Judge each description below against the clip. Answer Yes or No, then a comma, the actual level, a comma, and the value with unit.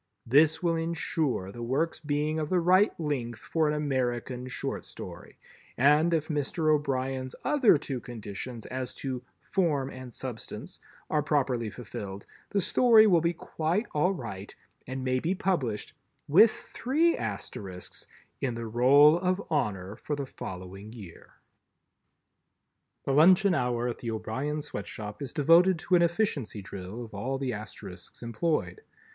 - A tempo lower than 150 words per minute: Yes, average, 140 wpm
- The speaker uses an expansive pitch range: Yes, wide, 5.7 semitones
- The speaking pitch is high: No, low, 135 Hz